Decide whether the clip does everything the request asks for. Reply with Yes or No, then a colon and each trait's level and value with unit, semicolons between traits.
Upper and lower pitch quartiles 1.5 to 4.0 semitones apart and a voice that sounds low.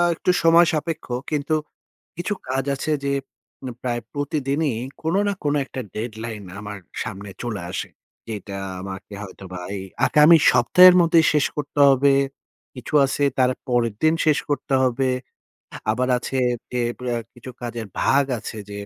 No: average, 5.1 semitones; low, 130 Hz